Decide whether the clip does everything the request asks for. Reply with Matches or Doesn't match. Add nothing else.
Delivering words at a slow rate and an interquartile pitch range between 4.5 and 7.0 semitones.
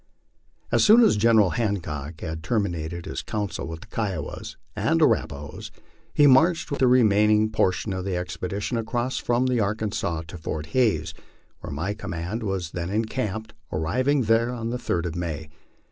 Doesn't match